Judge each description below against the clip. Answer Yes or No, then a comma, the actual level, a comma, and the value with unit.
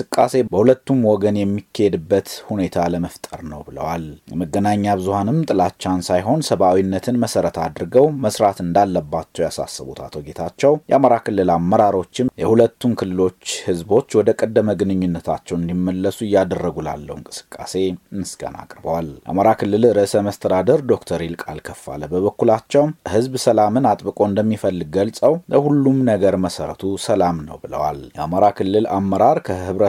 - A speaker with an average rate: No, fast, 115 wpm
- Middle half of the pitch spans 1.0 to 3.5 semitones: No, average, 4.2 semitones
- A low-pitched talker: Yes, low, 100 Hz